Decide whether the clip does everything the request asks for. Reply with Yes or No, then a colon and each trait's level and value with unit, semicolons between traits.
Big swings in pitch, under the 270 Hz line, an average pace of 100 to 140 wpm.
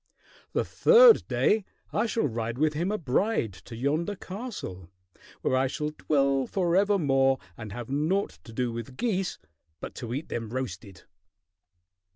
No: wide, 8.5 semitones; medium, 140 Hz; average, 150 wpm